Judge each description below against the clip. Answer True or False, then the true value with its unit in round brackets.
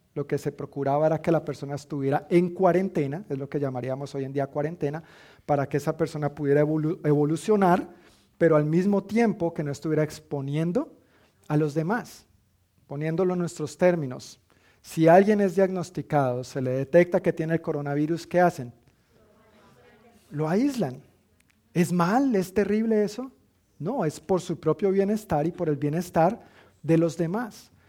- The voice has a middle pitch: True (155 Hz)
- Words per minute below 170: True (160 wpm)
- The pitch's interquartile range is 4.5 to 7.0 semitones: False (3.8 semitones)